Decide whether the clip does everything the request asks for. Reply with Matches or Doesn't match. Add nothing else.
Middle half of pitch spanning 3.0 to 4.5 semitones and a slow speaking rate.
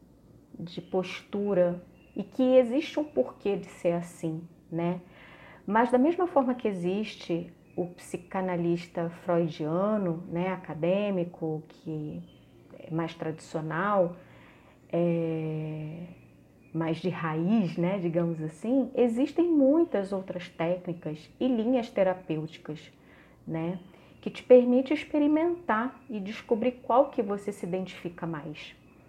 Doesn't match